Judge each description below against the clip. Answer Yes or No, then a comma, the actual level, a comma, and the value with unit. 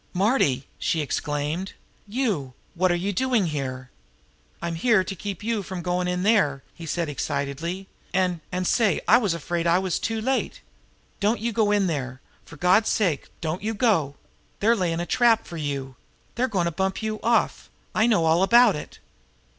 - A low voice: No, medium, 180 Hz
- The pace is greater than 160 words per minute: Yes, average, 180 wpm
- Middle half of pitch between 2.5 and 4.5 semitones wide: No, average, 4.9 semitones